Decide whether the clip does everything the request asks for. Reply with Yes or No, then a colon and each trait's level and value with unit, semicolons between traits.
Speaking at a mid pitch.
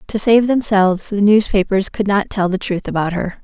No: high, 200 Hz